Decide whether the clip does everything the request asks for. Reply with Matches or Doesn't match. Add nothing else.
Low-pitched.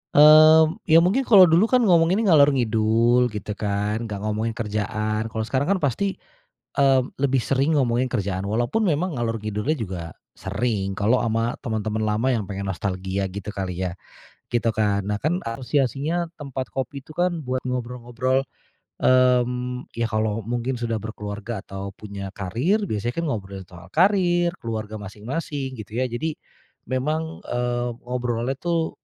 Matches